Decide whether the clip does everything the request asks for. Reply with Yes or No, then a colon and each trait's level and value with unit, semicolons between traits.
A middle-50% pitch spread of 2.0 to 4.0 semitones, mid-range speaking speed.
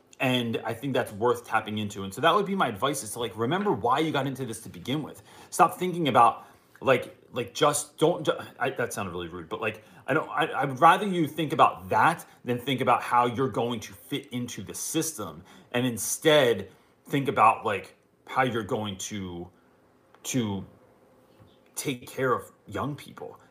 No: average, 4.9 semitones; average, 190 wpm